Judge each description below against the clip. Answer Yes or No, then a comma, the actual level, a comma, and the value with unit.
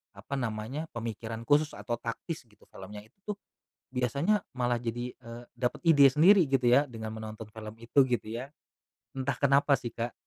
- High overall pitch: No, low, 125 Hz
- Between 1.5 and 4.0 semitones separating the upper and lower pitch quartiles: Yes, average, 3.7 semitones